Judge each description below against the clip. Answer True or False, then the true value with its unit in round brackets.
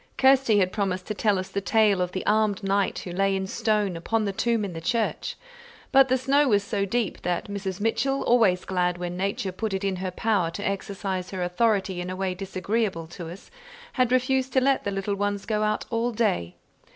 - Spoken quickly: True (215 wpm)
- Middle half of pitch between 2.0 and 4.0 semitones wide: True (3.3 semitones)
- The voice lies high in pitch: True (200 Hz)